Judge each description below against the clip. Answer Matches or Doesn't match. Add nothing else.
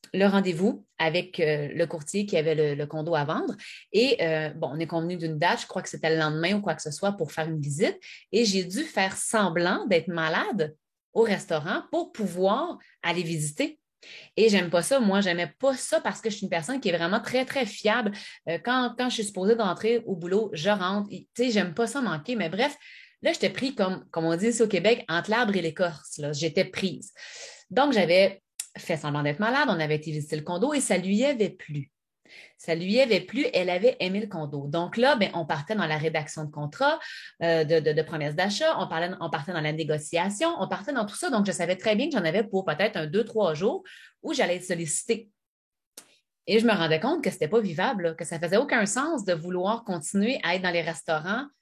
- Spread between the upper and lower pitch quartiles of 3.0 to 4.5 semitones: Doesn't match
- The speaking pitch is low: Doesn't match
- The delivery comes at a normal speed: Doesn't match